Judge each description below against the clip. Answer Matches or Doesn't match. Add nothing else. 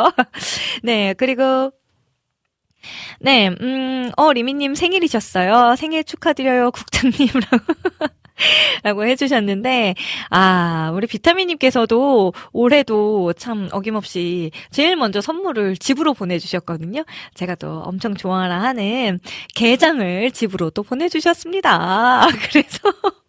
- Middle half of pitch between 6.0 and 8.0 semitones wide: Matches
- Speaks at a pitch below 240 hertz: Doesn't match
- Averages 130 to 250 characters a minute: Matches